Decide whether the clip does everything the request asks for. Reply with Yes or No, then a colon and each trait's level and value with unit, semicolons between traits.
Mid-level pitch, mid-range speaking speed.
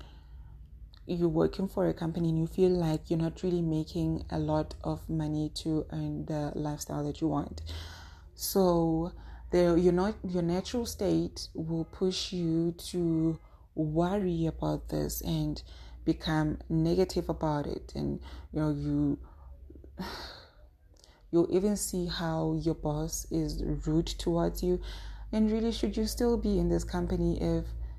Yes: medium, 160 Hz; average, 145 wpm